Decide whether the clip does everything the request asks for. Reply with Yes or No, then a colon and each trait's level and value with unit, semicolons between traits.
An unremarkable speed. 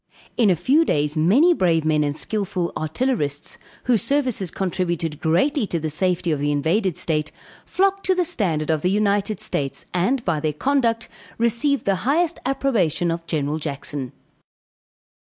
Yes: average, 155 wpm